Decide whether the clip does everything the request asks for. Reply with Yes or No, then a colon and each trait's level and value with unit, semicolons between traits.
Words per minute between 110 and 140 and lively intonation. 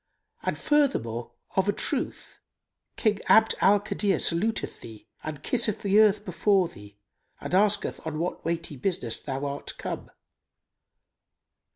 Yes: slow, 135 wpm; wide, 6.6 semitones